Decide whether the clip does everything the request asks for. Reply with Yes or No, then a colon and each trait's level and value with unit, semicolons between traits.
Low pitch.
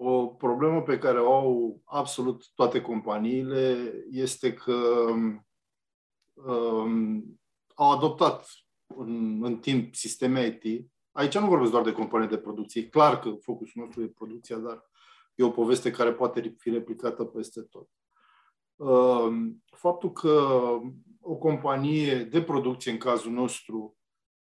Yes: low, 120 Hz